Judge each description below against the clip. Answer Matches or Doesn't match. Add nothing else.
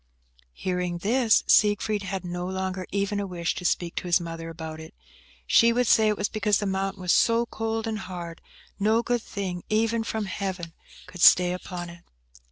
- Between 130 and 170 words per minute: Doesn't match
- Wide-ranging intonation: Doesn't match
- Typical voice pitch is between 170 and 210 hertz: Matches